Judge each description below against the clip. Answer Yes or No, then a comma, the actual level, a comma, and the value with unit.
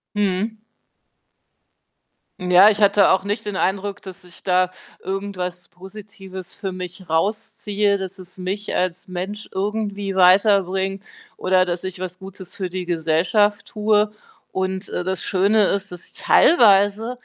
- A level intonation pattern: Yes, narrow, 1.9 semitones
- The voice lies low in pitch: No, high, 190 Hz